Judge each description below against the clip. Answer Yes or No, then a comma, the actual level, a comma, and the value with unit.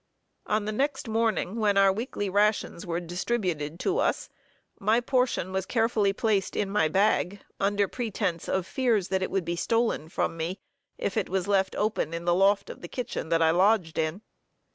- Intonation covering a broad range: No, average, 3.8 semitones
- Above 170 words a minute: Yes, average, 185 wpm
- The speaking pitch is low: No, high, 195 Hz